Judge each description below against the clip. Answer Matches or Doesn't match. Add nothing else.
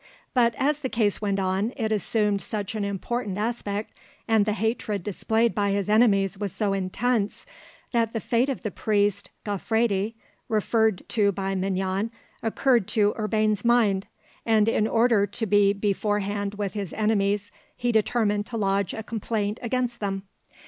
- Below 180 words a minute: Matches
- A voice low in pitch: Doesn't match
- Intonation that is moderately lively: Doesn't match